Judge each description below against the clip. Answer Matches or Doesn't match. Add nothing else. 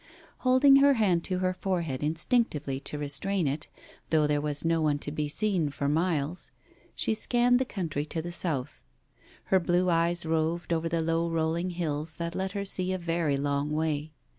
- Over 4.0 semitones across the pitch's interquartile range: Doesn't match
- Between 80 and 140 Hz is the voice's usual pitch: Doesn't match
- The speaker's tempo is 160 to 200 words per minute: Matches